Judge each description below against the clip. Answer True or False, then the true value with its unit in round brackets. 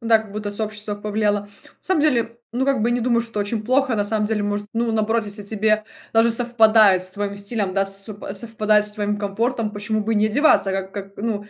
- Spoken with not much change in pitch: True (2.0 semitones)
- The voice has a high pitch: True (215 Hz)